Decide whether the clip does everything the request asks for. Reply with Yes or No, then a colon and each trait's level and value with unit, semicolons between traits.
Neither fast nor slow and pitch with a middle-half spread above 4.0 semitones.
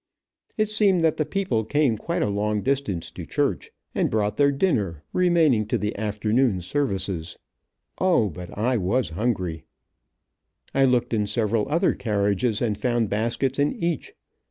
Yes: average, 155 wpm; wide, 5.5 semitones